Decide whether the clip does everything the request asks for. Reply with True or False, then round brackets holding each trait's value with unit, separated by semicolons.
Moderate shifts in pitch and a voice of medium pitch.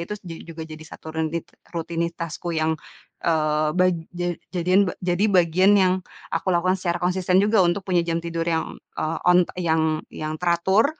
False (2.2 semitones; 170 Hz)